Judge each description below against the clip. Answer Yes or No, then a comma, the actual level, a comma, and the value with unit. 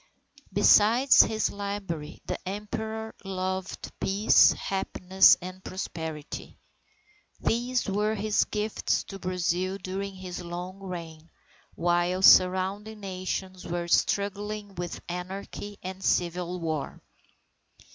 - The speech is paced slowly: Yes, slow, 100 wpm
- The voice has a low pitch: No, high, 190 Hz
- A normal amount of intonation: No, narrow, 2.3 semitones